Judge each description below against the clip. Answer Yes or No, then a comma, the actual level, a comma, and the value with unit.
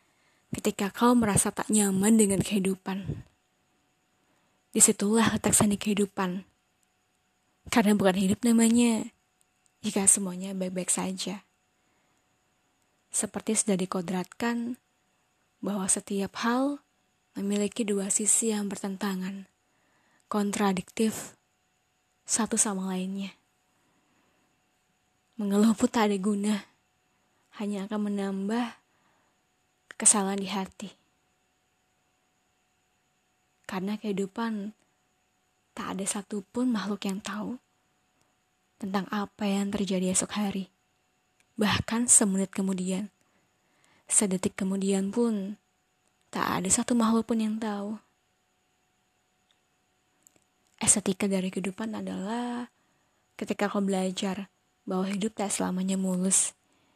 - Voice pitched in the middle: No, high, 200 Hz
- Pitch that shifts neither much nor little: No, narrow, 2.3 semitones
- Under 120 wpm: Yes, average, 90 wpm